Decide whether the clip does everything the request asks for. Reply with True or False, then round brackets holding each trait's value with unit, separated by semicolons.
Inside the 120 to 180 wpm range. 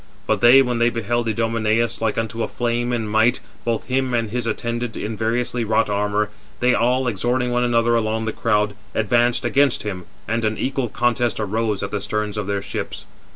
False (195 wpm)